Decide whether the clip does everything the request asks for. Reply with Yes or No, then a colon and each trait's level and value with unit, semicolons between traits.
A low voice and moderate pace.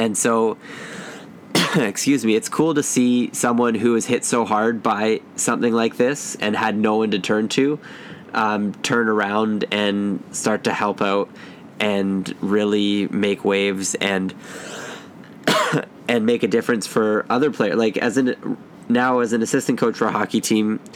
Yes: low, 110 Hz; average, 165 wpm